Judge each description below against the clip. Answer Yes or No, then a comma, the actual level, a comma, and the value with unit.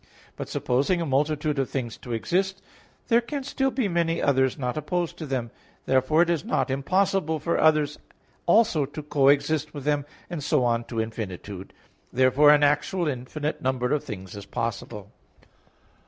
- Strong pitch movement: No, average, 4.6 semitones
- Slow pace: No, average, 165 wpm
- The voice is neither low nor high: Yes, medium, 145 Hz